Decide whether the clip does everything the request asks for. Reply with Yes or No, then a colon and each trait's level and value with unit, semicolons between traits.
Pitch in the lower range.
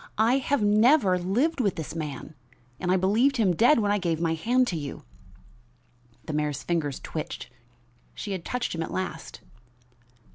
No: medium, 185 Hz